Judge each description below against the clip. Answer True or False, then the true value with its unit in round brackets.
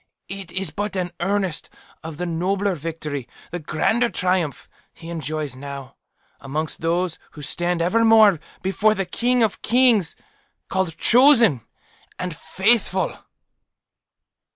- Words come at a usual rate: False (120 wpm)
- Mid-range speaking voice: True (180 Hz)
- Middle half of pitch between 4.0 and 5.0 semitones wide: True (4.3 semitones)